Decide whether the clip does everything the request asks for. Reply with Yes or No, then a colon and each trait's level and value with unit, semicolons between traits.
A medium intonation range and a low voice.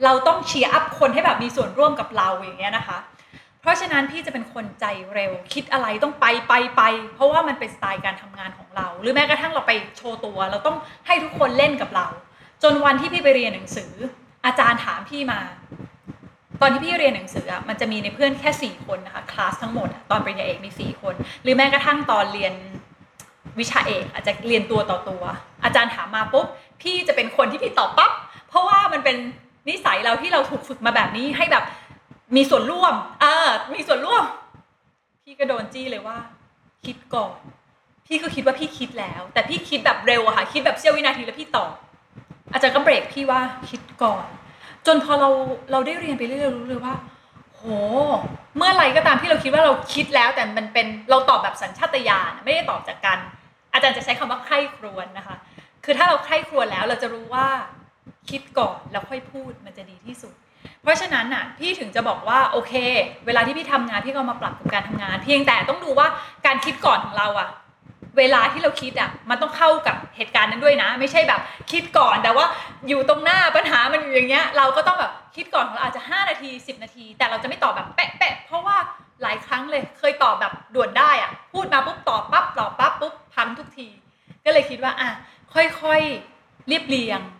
No: average, 4.4 semitones; very high, 270 Hz